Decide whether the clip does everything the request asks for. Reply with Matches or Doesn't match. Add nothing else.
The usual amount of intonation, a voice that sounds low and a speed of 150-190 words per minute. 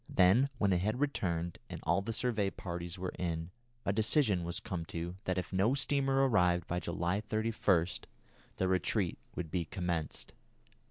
Matches